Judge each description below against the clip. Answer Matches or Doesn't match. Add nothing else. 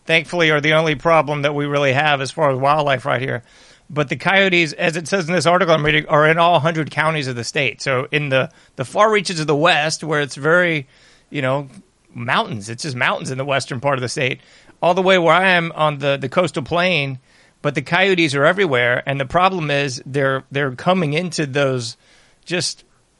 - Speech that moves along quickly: Matches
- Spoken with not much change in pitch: Doesn't match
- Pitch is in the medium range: Matches